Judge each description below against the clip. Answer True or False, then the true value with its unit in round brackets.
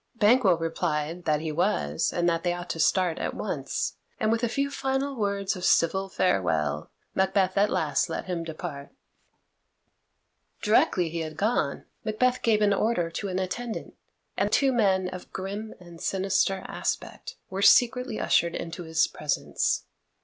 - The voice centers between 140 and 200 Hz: True (185 Hz)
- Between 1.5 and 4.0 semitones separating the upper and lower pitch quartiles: False (4.5 semitones)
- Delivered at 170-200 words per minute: False (155 wpm)